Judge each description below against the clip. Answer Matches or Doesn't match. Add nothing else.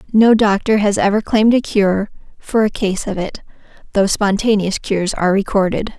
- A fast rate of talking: Doesn't match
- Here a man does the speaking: Doesn't match